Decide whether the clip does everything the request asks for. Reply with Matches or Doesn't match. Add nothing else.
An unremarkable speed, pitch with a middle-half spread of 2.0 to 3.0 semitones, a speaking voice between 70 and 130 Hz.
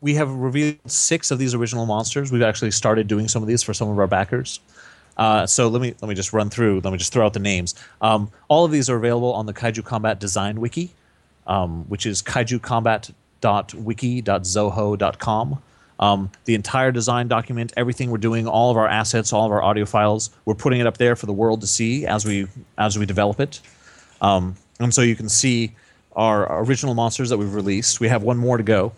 Doesn't match